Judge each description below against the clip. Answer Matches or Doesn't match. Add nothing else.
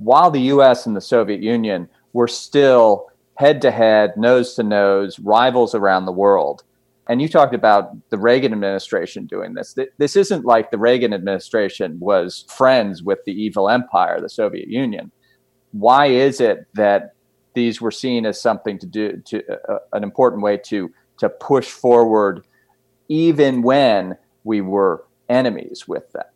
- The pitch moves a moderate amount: Matches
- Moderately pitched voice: Doesn't match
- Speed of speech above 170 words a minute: Doesn't match